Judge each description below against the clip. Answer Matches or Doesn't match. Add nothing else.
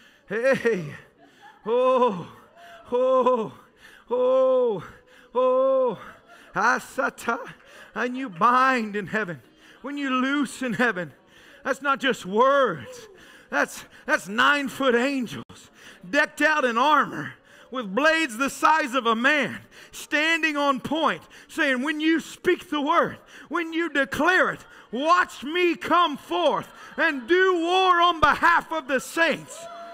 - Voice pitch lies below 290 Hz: Doesn't match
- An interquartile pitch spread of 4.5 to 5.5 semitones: Matches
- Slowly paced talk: Matches